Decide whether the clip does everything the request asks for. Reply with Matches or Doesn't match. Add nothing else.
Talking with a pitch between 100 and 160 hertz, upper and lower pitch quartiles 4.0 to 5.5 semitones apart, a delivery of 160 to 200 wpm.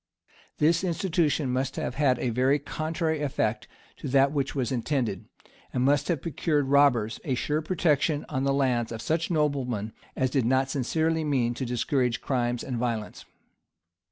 Doesn't match